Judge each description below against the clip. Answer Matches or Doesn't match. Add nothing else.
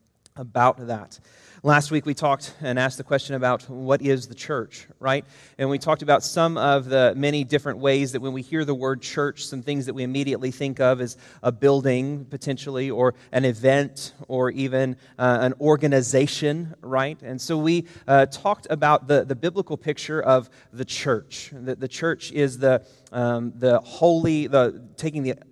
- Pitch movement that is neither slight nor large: Doesn't match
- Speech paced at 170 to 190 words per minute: Matches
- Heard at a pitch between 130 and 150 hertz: Matches